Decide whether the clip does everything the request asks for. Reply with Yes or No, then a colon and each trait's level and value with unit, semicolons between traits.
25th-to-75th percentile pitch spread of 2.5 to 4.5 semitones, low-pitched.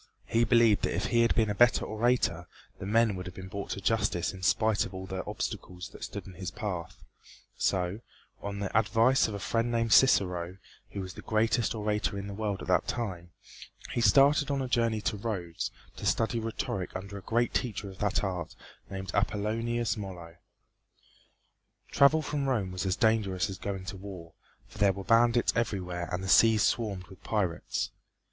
Yes: average, 3.5 semitones; low, 105 Hz